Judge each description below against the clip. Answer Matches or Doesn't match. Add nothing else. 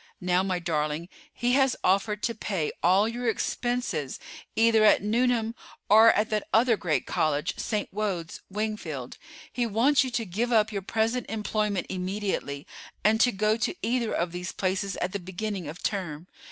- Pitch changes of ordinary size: Matches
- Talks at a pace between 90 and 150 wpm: Doesn't match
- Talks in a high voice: Matches